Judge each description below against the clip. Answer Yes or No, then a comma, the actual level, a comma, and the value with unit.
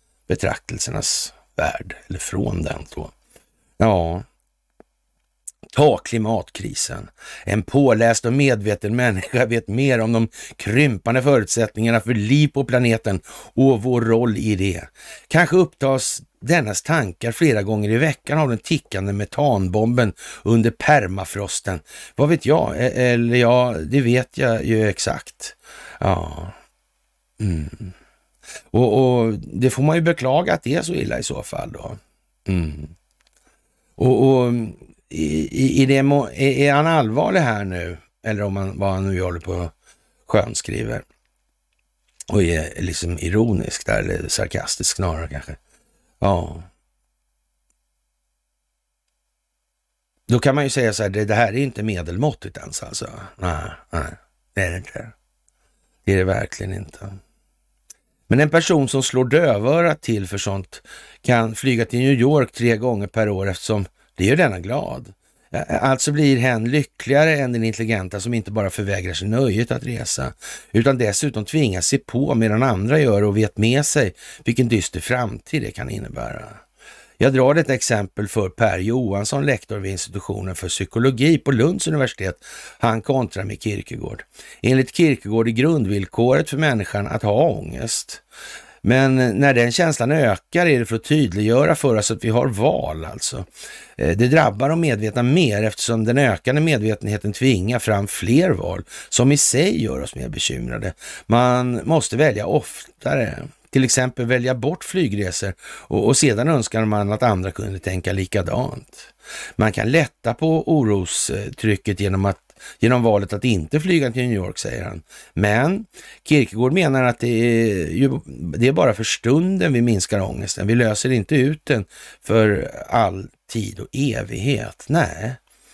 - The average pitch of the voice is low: Yes, low, 115 Hz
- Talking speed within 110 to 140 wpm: No, average, 150 wpm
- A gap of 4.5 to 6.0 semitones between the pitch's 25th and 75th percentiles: Yes, average, 4.9 semitones